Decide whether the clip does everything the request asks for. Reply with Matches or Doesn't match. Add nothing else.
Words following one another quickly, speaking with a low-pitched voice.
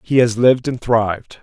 Matches